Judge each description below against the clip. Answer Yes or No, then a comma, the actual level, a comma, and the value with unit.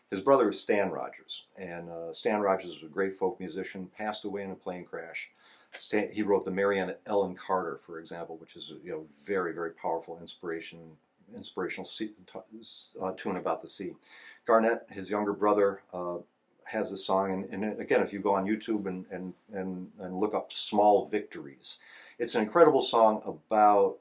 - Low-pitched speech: Yes, very low, 95 Hz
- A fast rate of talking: No, average, 185 wpm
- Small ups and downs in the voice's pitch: Yes, narrow, 2.3 semitones